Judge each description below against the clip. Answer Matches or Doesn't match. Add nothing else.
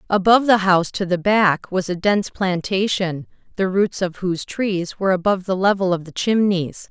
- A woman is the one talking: Matches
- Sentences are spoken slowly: Doesn't match